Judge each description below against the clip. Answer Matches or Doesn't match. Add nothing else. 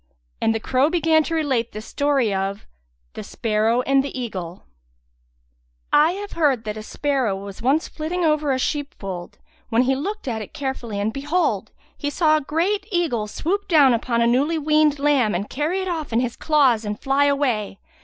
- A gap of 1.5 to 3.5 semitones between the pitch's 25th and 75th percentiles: Doesn't match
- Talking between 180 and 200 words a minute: Matches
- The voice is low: Doesn't match